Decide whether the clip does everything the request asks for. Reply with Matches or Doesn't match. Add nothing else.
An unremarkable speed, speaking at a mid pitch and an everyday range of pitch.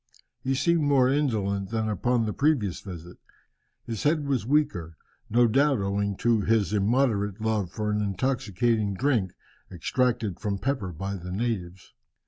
Doesn't match